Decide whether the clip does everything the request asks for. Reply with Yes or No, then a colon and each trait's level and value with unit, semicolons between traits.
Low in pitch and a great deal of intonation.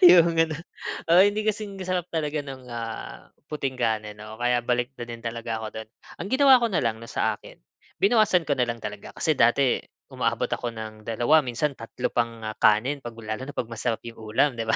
Yes: low, 120 Hz; wide, 5.7 semitones